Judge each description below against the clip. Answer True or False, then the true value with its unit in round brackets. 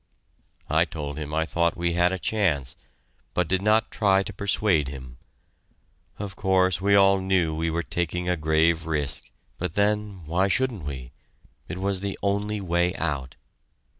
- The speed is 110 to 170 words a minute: True (165 wpm)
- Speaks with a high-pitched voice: False (90 Hz)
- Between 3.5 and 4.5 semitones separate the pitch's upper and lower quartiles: True (3.8 semitones)